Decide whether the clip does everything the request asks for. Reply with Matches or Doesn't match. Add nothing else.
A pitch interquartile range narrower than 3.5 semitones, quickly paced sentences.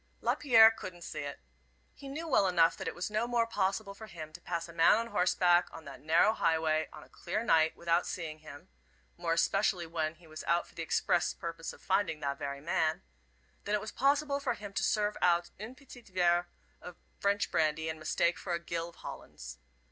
Doesn't match